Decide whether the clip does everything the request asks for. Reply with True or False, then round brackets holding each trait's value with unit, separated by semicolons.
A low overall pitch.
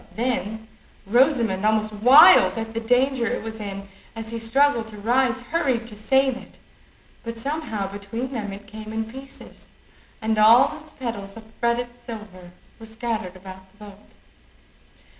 False (225 Hz)